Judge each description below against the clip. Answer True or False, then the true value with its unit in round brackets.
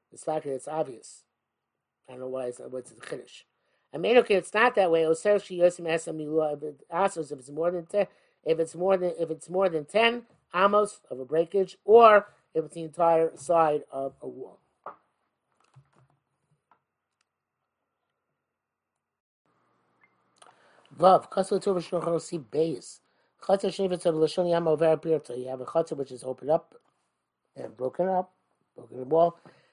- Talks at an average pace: False (120 wpm)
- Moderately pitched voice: True (165 Hz)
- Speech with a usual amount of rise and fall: True (4.2 semitones)